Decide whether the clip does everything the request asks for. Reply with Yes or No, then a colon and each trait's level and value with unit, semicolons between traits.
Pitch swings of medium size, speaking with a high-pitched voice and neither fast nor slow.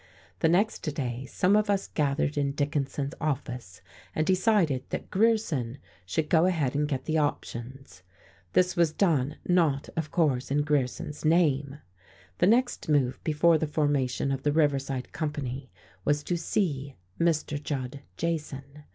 No: average, 3.4 semitones; medium, 150 Hz; average, 145 wpm